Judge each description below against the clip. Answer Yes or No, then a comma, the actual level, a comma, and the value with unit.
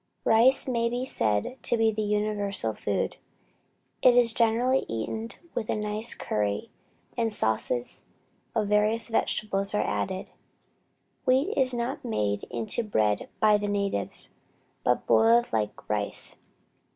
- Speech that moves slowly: Yes, slow, 130 wpm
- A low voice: No, high, 210 Hz